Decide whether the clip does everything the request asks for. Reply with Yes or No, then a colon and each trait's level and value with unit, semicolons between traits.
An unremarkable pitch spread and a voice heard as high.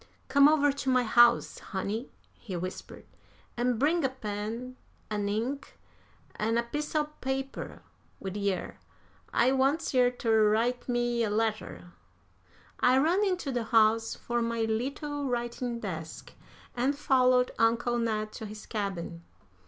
Yes: average, 3.5 semitones; high, 240 Hz